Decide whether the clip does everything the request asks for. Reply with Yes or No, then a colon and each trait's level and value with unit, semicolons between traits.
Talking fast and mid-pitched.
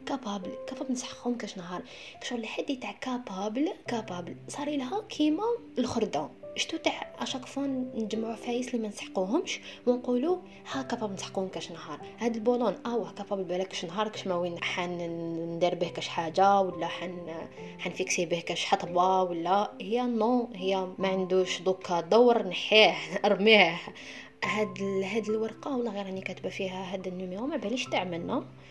No: fast, 150 wpm; high, 200 Hz